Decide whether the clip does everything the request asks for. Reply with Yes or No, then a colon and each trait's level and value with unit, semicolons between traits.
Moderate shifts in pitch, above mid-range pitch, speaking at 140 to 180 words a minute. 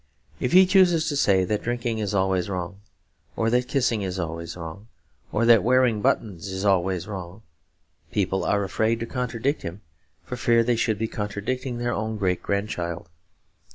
No: average, 4.1 semitones; low, 105 Hz; average, 170 wpm